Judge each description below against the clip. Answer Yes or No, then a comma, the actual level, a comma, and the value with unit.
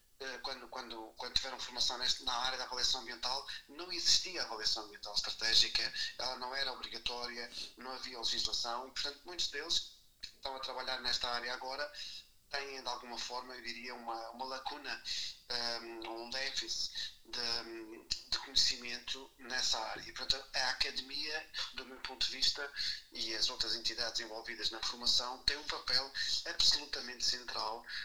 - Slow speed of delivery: No, average, 150 wpm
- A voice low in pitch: Yes, low, 125 Hz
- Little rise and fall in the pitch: Yes, narrow, 2.1 semitones